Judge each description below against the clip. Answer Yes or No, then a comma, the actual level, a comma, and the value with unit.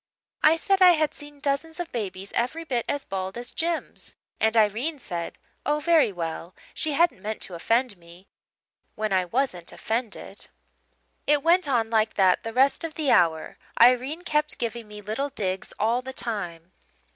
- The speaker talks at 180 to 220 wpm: No, average, 170 wpm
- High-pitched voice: Yes, high, 240 Hz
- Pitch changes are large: Yes, wide, 7.0 semitones